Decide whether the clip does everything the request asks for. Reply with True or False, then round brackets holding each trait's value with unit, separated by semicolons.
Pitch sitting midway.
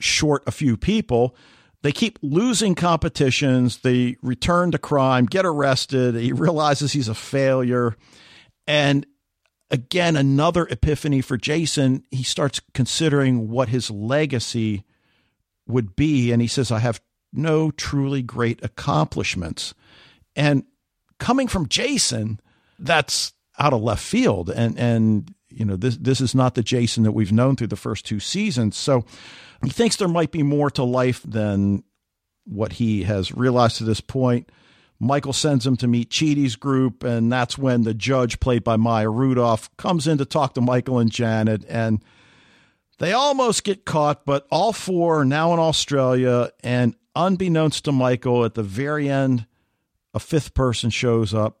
False (130 Hz)